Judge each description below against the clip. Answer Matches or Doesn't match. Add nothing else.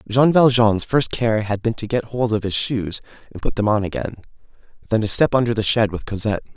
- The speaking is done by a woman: Doesn't match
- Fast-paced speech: Matches